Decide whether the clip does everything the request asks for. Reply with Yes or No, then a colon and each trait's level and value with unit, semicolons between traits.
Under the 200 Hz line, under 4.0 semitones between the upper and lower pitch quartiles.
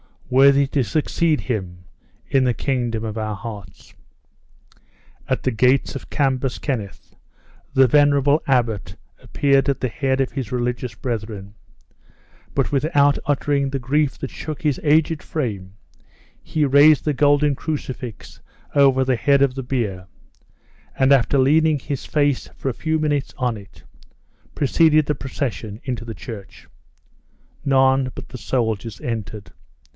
Yes: low, 135 Hz; average, 3.6 semitones